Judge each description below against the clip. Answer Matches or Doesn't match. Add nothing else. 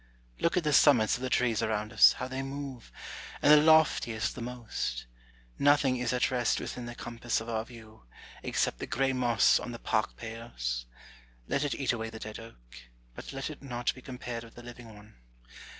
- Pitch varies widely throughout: Doesn't match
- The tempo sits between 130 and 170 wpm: Doesn't match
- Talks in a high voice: Doesn't match